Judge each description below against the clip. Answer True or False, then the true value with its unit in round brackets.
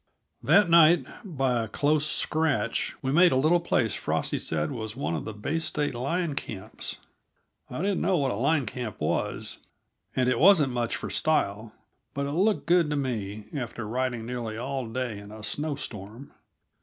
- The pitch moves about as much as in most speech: False (5.7 semitones)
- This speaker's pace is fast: False (180 wpm)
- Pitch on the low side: True (130 Hz)